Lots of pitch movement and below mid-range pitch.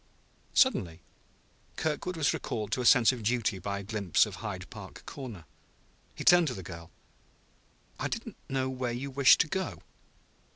Yes: wide, 5.7 semitones; low, 125 Hz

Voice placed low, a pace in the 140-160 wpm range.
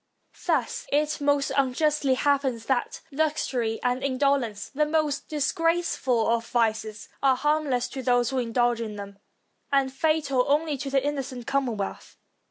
No: very high, 270 Hz; average, 145 wpm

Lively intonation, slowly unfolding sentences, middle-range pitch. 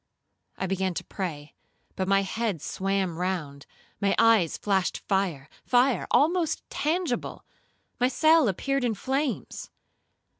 No: wide, 5.8 semitones; slow, 115 wpm; high, 195 Hz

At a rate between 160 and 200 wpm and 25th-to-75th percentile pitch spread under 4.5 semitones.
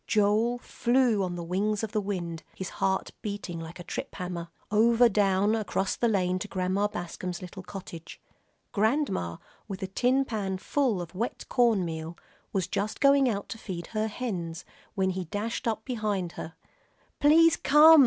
Yes: average, 170 wpm; average, 3.9 semitones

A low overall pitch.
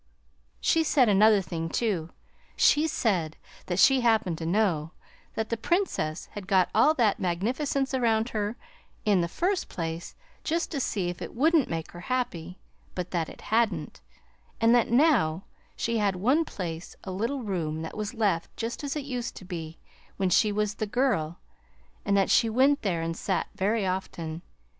No: high, 205 Hz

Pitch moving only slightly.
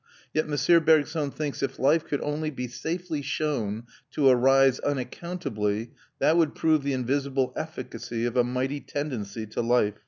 No: average, 3.8 semitones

